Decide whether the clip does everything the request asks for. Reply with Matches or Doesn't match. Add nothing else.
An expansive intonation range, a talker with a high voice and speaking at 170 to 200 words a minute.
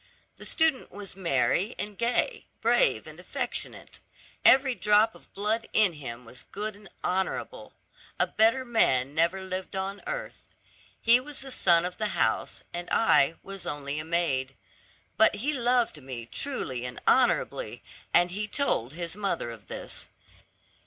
Doesn't match